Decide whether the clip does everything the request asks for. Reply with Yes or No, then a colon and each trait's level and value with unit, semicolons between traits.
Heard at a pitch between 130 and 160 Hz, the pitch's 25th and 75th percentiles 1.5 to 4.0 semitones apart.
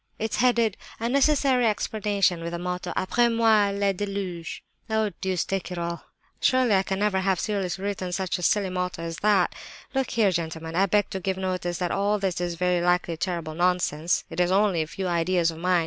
No: medium, 185 Hz; average, 2.8 semitones